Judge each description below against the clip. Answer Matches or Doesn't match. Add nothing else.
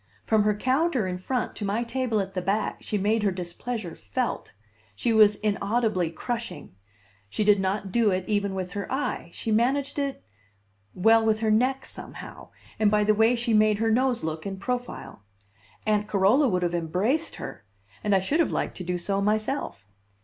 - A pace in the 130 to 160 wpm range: Doesn't match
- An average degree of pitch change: Matches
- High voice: Matches